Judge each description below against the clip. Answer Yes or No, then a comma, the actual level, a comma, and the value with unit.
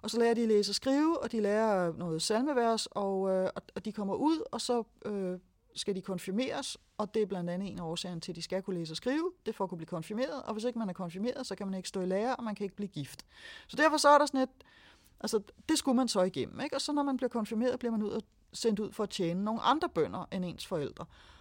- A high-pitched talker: Yes, high, 215 Hz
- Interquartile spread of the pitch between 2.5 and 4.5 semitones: No, average, 5.0 semitones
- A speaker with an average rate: No, fast, 280 wpm